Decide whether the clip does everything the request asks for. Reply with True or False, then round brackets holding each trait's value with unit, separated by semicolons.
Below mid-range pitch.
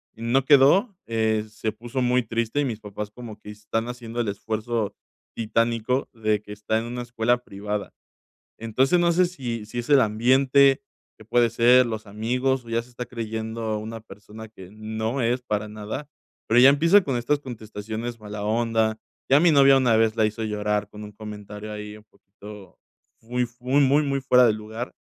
True (115 Hz)